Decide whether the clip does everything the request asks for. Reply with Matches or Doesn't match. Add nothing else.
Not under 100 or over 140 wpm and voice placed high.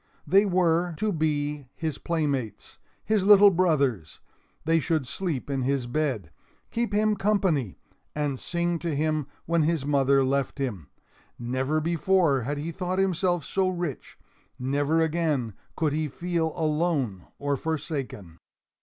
Doesn't match